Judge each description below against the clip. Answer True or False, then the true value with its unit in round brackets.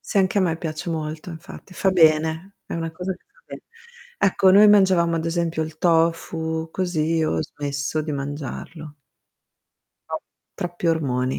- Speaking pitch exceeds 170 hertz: False (165 Hz)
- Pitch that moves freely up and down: False (2.4 semitones)